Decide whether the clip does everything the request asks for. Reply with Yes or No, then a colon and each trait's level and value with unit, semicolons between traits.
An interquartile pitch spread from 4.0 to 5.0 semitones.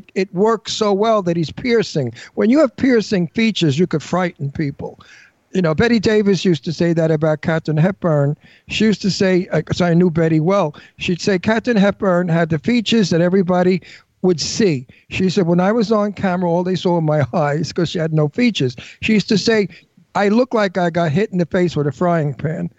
Yes: average, 4.3 semitones